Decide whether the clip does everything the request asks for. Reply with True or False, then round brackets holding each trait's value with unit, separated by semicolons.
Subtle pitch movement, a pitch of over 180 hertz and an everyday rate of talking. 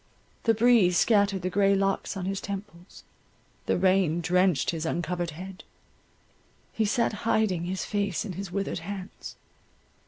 True (2.2 semitones; 190 Hz; 145 wpm)